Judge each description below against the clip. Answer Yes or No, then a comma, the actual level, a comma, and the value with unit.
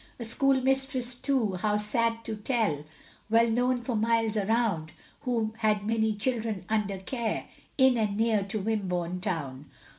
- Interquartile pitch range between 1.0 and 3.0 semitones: Yes, average, 2.7 semitones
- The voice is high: Yes, high, 220 Hz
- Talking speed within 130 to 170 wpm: Yes, average, 145 wpm